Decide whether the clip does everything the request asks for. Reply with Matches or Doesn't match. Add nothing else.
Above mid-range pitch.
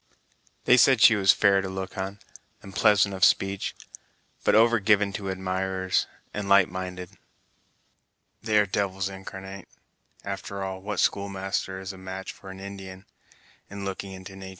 Doesn't match